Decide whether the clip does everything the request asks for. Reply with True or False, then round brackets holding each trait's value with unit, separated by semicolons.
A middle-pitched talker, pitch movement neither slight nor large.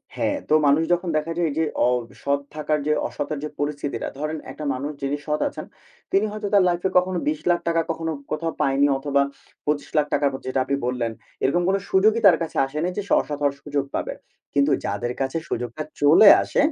True (150 Hz; 3.4 semitones)